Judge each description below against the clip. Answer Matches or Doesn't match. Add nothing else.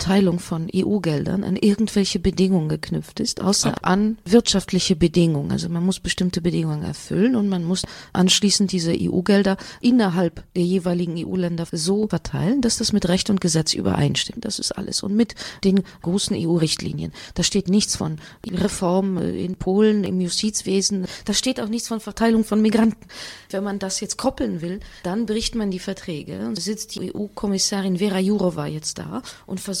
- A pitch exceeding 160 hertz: Matches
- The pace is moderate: Matches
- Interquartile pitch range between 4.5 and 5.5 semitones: Doesn't match